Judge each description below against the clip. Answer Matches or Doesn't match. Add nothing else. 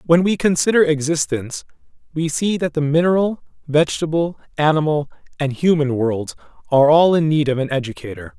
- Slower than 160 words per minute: Matches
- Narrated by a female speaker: Doesn't match